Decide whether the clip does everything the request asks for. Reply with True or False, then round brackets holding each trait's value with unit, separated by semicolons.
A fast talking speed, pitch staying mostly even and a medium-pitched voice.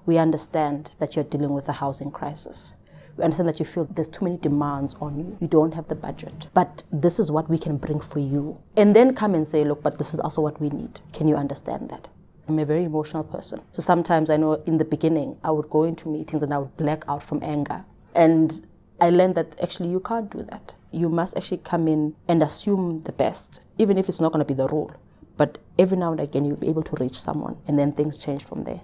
True (250 wpm; 2.2 semitones; 155 Hz)